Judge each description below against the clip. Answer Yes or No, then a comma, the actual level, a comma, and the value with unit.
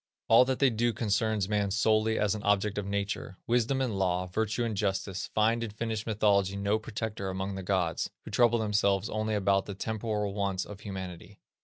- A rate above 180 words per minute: Yes, average, 190 wpm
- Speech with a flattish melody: Yes, narrow, 2.2 semitones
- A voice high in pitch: No, low, 105 Hz